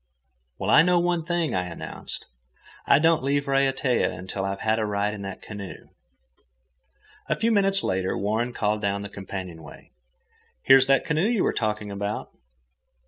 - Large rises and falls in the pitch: Yes, wide, 7.1 semitones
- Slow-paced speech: No, average, 160 wpm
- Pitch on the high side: No, low, 110 Hz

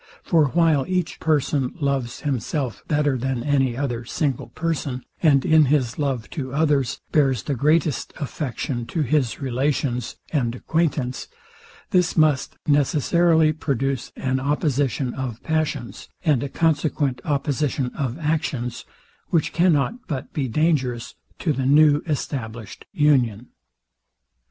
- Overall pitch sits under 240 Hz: Yes, medium, 140 Hz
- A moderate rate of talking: No, slow, 125 wpm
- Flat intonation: No, average, 3.3 semitones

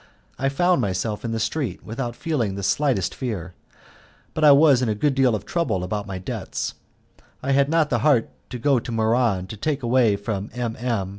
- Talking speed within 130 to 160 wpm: No, fast, 205 wpm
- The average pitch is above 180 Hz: No, low, 120 Hz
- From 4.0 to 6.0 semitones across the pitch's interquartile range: Yes, average, 5.0 semitones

